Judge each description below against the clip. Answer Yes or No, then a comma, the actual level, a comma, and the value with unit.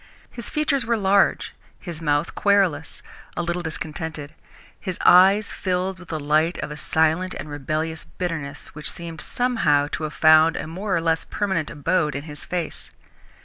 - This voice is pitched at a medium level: Yes, medium, 165 Hz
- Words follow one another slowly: No, average, 165 wpm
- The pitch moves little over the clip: No, average, 3.2 semitones